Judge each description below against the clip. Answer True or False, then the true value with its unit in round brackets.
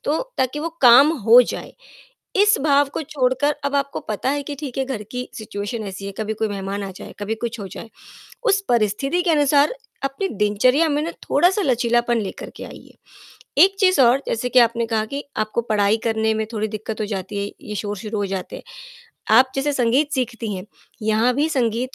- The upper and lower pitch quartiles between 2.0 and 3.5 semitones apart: False (4.7 semitones)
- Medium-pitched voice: False (240 Hz)